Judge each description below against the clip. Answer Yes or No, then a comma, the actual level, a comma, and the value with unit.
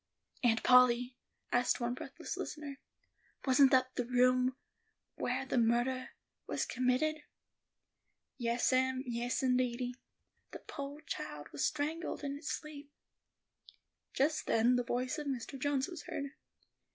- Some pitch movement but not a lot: No, narrow, 2.3 semitones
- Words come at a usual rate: No, slow, 130 wpm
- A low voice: No, very high, 255 Hz